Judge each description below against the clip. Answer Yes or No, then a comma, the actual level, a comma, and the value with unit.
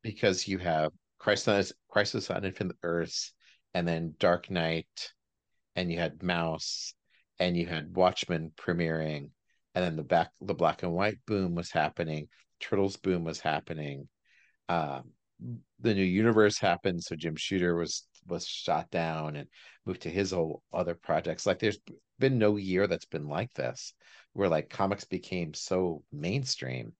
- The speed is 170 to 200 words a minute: No, average, 155 wpm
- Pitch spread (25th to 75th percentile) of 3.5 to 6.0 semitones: No, average, 2.8 semitones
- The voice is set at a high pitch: No, very low, 85 Hz